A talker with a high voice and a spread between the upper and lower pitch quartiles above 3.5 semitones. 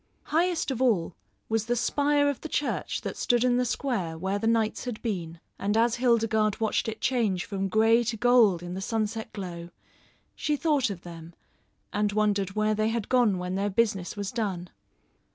Yes: high, 215 Hz; average, 3.9 semitones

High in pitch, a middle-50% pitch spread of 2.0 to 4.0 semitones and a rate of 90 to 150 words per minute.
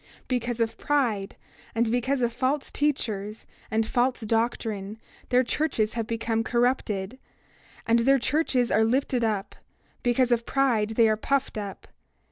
Yes: high, 235 Hz; average, 2.7 semitones; average, 145 wpm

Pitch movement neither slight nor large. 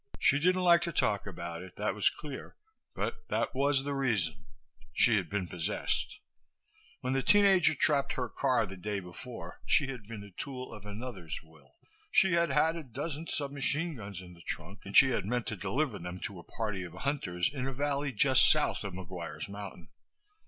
No: wide, 7.2 semitones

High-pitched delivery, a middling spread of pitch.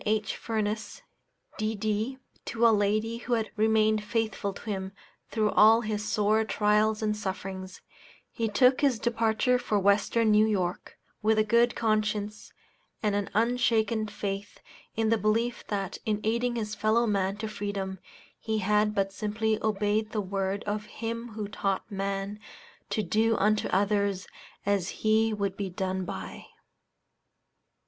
No: high, 215 Hz; narrow, 1.6 semitones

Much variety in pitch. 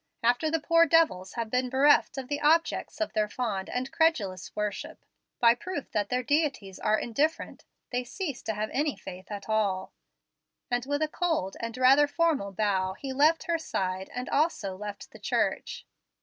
Yes: wide, 6.5 semitones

